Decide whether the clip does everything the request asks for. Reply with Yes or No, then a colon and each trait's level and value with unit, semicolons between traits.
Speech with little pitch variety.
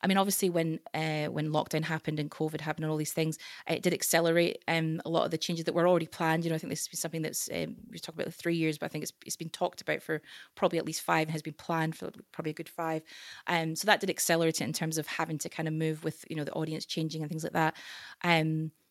Yes: narrow, 1.1 semitones